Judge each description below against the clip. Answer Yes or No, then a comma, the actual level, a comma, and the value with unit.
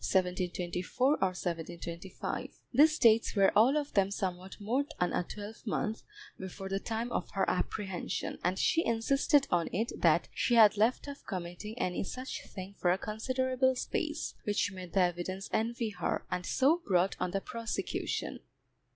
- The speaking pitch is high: Yes, high, 205 Hz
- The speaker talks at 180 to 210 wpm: No, average, 150 wpm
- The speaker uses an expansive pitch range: No, average, 4.7 semitones